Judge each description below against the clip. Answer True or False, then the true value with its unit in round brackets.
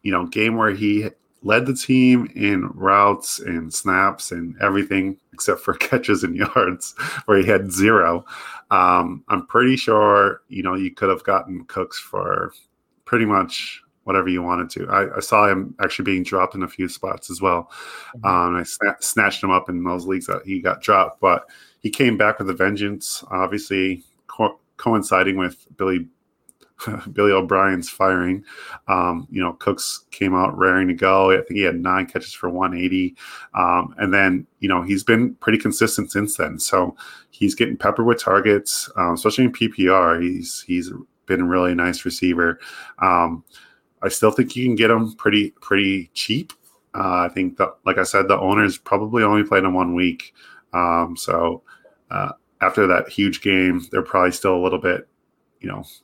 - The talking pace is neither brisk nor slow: True (180 wpm)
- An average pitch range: False (2.3 semitones)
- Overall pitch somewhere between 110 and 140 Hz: False (95 Hz)